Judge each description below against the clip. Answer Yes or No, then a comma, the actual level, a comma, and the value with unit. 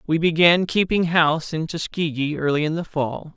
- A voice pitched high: No, medium, 160 Hz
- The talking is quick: No, average, 180 wpm